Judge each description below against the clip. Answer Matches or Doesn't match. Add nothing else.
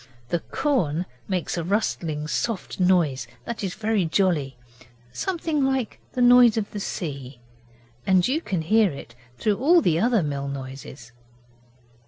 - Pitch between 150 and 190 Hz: Matches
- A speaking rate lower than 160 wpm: Matches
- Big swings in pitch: Matches